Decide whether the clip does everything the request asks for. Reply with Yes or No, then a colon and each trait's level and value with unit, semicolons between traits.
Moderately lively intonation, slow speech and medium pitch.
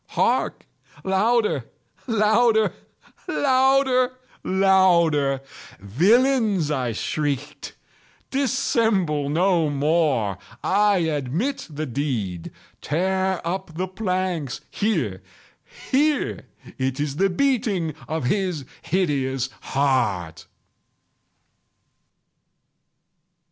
No: wide, 7.0 semitones; slow, 65 wpm; medium, 175 Hz